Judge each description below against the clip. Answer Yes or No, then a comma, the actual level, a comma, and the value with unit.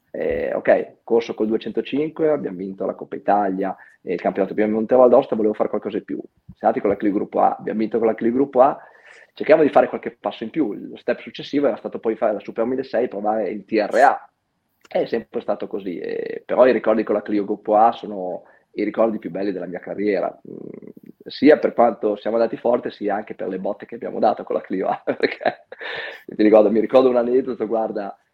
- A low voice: Yes, low, 115 Hz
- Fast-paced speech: Yes, fast, 220 wpm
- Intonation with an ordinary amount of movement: Yes, average, 3.1 semitones